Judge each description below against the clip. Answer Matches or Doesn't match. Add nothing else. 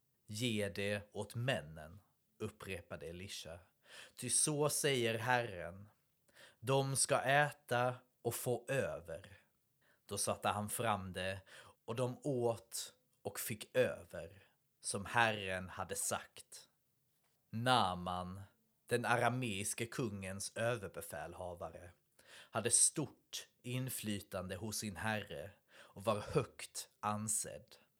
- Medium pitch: Doesn't match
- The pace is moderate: Doesn't match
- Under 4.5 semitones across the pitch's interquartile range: Matches